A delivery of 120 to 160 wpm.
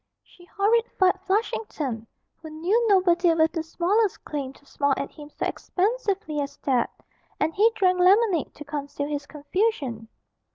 Yes: average, 150 wpm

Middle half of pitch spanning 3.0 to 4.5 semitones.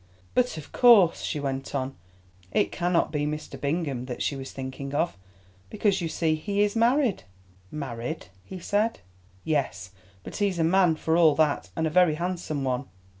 No: average, 4.9 semitones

